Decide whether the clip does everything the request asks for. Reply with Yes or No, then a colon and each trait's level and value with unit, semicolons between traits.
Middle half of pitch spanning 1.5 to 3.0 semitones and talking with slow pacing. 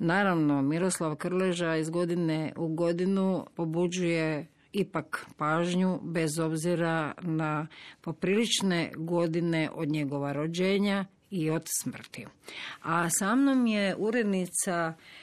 Yes: narrow, 2.6 semitones; slow, 100 wpm